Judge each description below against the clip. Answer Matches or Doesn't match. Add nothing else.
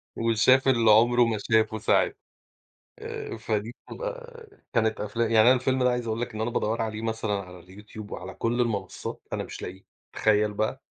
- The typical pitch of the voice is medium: Doesn't match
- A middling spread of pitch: Doesn't match